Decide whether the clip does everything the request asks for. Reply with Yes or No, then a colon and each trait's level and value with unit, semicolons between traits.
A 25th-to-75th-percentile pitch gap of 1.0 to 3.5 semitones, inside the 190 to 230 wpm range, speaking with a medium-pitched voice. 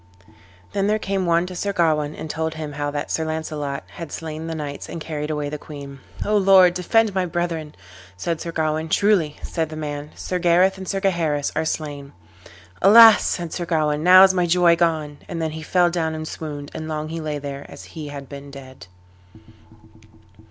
Yes: average, 3.1 semitones; average, 200 wpm; medium, 160 Hz